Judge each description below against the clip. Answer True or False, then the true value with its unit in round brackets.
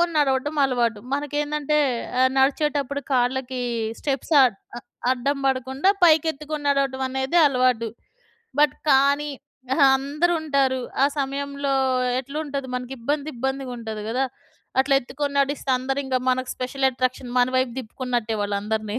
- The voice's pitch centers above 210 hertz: True (270 Hz)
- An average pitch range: False (2.1 semitones)